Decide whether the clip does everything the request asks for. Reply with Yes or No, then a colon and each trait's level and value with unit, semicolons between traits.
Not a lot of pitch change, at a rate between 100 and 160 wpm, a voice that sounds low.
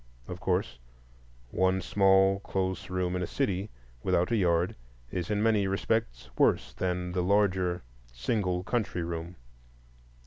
Yes: narrow, 1.7 semitones; slow, 135 wpm; very low, 95 Hz